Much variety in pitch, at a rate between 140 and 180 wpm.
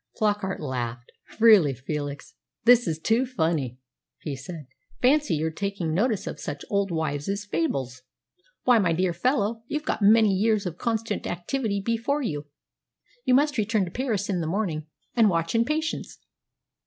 Yes: wide, 6.2 semitones; average, 160 wpm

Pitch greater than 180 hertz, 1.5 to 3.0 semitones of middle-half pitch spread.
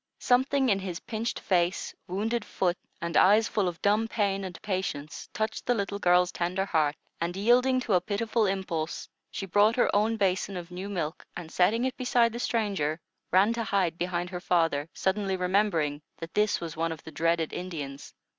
No: high, 190 Hz; average, 3.8 semitones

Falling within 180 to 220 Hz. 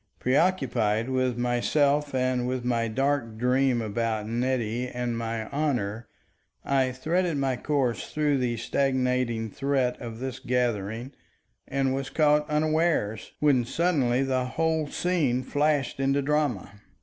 No: low, 130 Hz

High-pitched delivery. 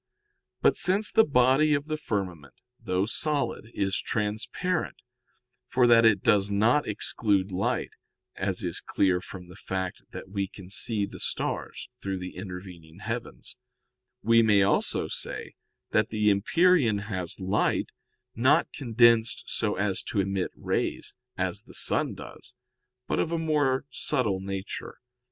No: low, 105 Hz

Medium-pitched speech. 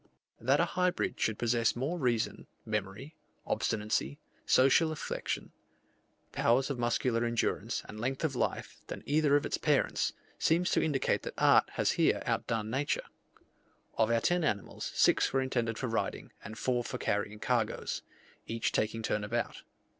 No: low, 120 Hz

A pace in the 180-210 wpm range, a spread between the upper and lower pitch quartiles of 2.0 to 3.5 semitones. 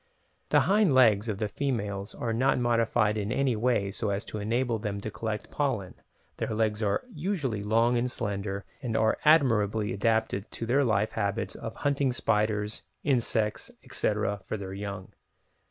No: average, 170 wpm; average, 3.0 semitones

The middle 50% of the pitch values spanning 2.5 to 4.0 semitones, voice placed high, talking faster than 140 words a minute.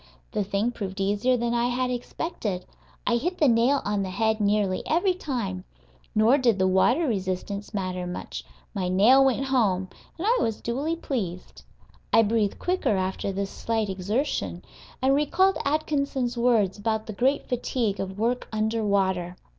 No: average, 4.7 semitones; high, 225 Hz; average, 160 wpm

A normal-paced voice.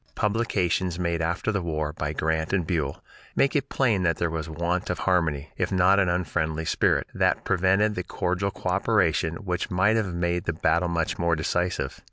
Yes: average, 185 wpm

